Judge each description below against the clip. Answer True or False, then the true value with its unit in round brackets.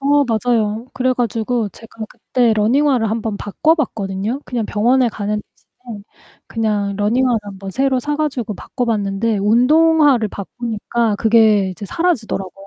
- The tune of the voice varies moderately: True (3.5 semitones)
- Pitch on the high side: True (225 Hz)